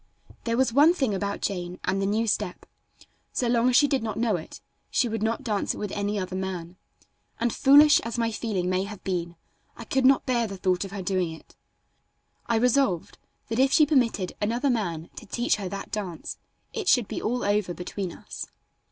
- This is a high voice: Yes, high, 210 Hz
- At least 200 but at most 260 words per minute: Yes, fast, 205 wpm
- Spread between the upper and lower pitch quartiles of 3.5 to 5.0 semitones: Yes, average, 4.5 semitones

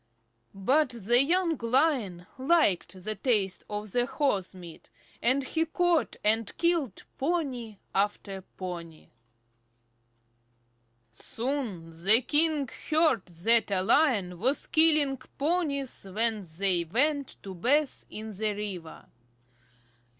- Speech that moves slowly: Yes, slow, 110 wpm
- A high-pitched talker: Yes, high, 230 Hz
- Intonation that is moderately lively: No, wide, 6.9 semitones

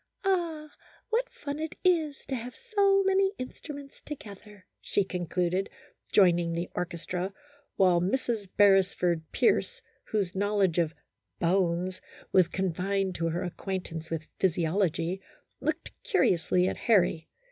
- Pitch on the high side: Yes, high, 195 Hz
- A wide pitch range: Yes, wide, 8.2 semitones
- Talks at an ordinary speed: No, slow, 130 wpm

